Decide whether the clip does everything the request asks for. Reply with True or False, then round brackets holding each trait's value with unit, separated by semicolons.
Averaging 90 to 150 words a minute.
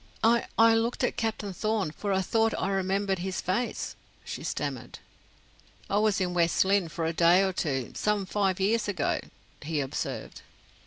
False (170 wpm)